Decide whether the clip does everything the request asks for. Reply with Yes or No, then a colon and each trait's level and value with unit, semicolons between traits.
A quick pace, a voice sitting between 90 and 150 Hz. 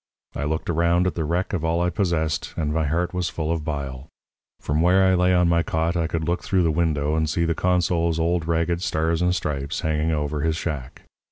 No: fast, 230 wpm; very low, 80 Hz